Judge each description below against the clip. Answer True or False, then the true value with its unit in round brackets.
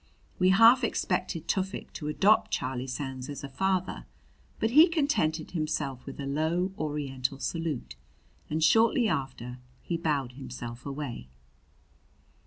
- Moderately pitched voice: True (155 Hz)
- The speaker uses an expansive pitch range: True (5.8 semitones)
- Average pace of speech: False (130 wpm)